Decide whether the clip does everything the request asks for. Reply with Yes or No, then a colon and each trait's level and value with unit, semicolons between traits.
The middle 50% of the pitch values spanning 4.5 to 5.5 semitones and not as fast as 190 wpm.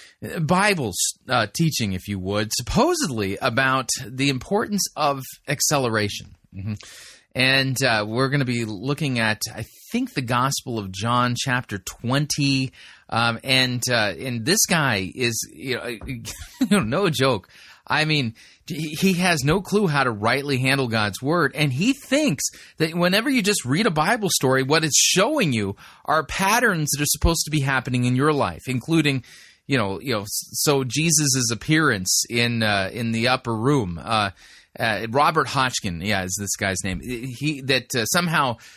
Yes: average, 5.2 semitones; average, 165 wpm